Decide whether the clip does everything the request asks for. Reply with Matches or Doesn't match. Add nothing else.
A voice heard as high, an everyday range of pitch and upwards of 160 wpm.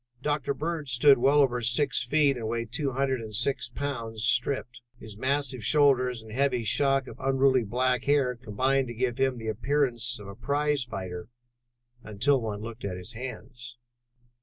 Doesn't match